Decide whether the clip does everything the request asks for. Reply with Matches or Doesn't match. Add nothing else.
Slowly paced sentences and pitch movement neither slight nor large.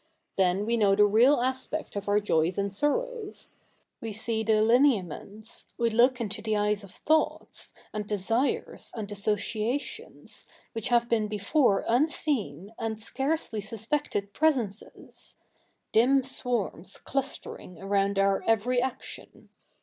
Matches